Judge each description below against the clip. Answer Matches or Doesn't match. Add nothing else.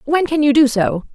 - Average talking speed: Doesn't match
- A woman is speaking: Matches